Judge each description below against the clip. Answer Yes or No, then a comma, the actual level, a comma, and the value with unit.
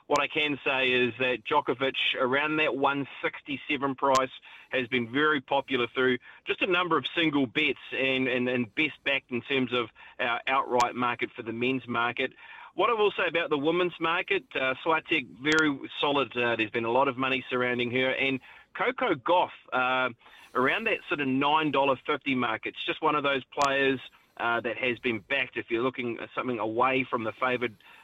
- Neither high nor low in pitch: No, low, 130 Hz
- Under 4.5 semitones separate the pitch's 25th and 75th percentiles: Yes, average, 3.1 semitones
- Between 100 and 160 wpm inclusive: No, average, 190 wpm